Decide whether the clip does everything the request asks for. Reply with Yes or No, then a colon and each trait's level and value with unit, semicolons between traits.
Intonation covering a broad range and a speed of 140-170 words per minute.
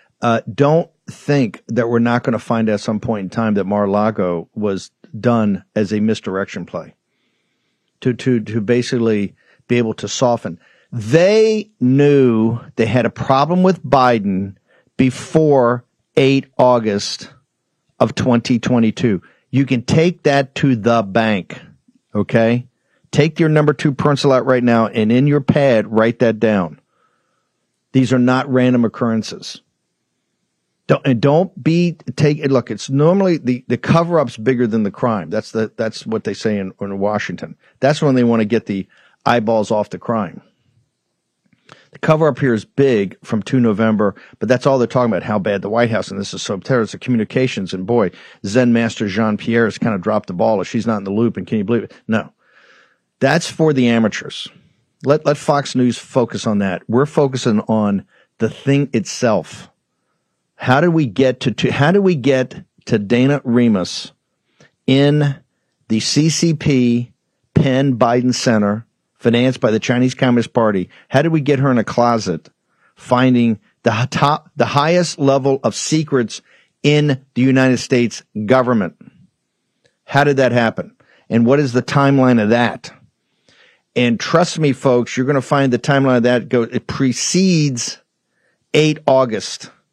No: average, 3.8 semitones; average, 165 wpm